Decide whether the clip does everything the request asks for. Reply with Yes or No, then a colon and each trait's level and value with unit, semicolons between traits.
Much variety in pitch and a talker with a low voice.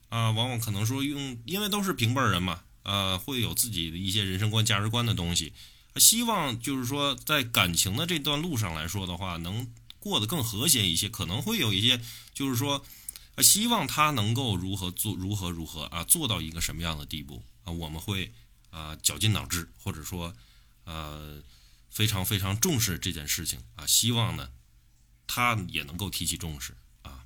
Yes: wide, 6.4 semitones; low, 100 Hz